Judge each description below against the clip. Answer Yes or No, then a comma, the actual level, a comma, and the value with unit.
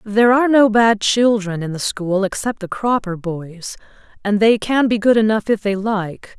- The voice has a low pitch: No, high, 210 Hz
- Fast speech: No, average, 190 wpm